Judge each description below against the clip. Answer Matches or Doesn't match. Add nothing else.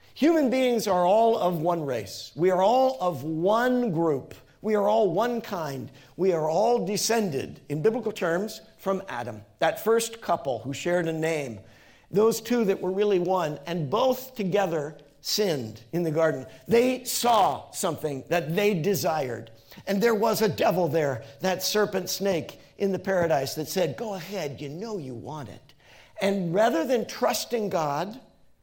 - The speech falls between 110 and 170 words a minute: Matches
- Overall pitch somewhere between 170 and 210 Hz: Matches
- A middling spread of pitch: Doesn't match